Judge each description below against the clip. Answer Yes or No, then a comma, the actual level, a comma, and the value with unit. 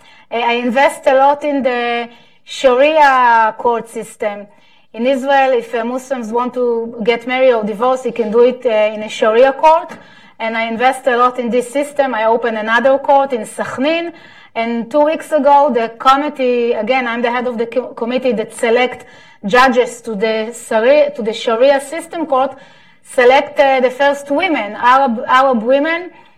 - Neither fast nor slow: Yes, average, 170 wpm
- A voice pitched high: Yes, very high, 250 Hz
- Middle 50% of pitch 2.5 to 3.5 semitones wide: Yes, average, 3.2 semitones